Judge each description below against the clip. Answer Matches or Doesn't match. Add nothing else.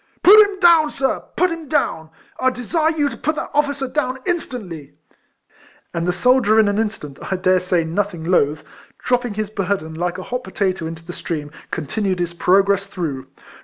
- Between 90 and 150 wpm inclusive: Doesn't match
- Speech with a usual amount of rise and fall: Doesn't match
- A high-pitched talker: Matches